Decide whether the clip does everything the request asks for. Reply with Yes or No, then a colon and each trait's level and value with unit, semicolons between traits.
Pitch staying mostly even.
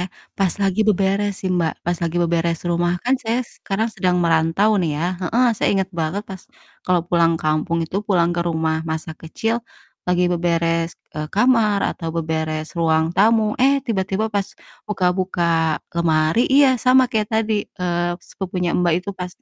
No: average, 3.7 semitones